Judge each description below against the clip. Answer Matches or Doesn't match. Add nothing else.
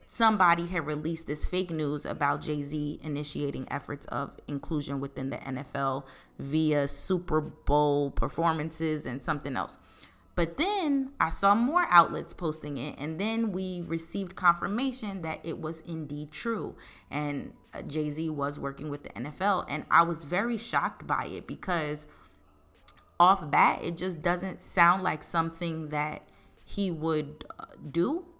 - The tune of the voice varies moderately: Matches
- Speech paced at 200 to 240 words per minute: Doesn't match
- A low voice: Doesn't match